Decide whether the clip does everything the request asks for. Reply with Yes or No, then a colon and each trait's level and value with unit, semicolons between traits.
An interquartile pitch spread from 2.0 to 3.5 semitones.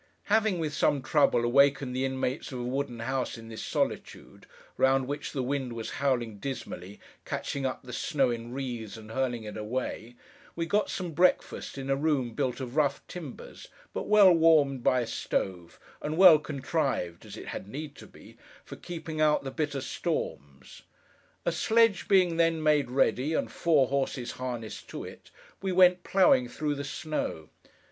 No: average, 4.3 semitones